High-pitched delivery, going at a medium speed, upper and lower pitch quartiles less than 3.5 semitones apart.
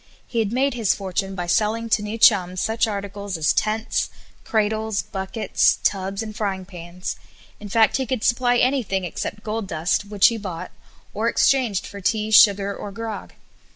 Yes: high, 210 Hz; average, 170 wpm; narrow, 2.6 semitones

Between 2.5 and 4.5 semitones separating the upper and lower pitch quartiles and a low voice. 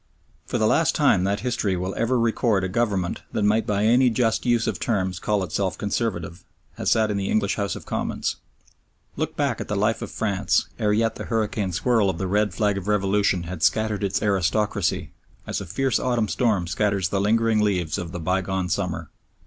Yes: average, 2.9 semitones; low, 100 Hz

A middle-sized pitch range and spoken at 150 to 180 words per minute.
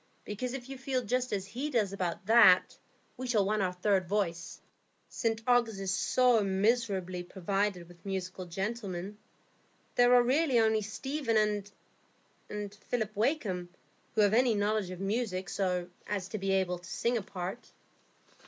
Yes: average, 3.9 semitones; average, 155 wpm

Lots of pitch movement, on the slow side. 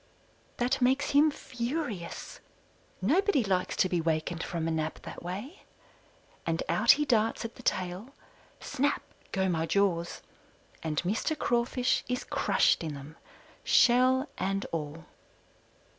Yes: wide, 7.3 semitones; slow, 130 wpm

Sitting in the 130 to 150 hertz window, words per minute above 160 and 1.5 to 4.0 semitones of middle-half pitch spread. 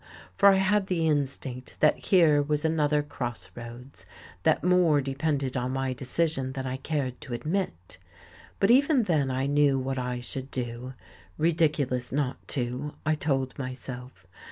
No: medium, 140 Hz; average, 155 wpm; average, 3.5 semitones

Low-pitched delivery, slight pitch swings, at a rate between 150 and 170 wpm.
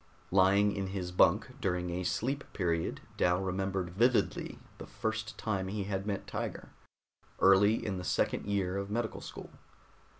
Yes: very low, 95 Hz; narrow, 2.2 semitones; average, 155 wpm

